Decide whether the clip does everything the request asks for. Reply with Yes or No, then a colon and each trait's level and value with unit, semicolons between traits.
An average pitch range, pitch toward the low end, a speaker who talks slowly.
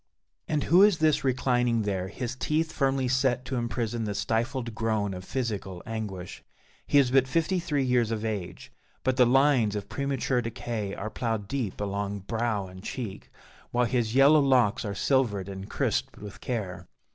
No: average, 4.3 semitones; low, 120 Hz; average, 170 wpm